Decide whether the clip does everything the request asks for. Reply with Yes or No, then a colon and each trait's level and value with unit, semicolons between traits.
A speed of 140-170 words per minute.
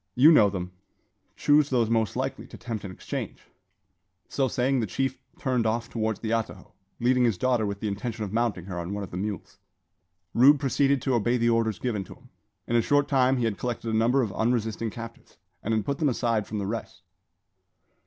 No: fast, 205 wpm